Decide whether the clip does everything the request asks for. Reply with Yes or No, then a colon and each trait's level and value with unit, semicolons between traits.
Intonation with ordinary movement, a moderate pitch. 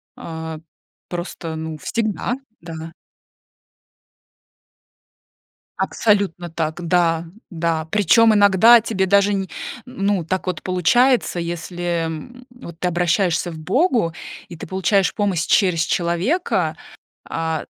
Yes: average, 3.7 semitones; medium, 180 Hz